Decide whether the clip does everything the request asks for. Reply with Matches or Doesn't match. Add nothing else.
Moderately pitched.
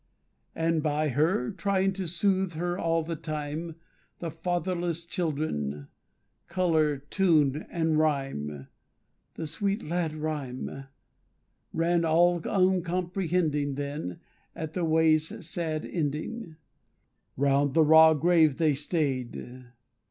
Matches